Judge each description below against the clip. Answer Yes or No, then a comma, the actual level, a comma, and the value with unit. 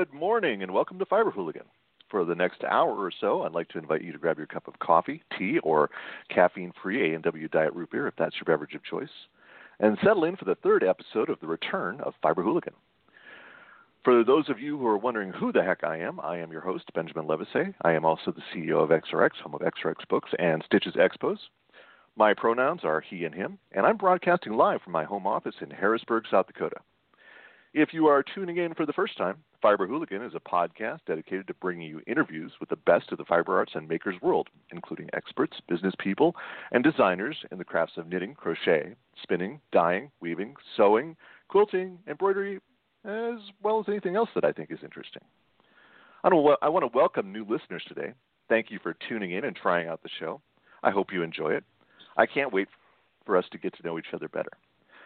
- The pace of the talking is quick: Yes, fast, 210 wpm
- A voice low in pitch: Yes, low, 125 Hz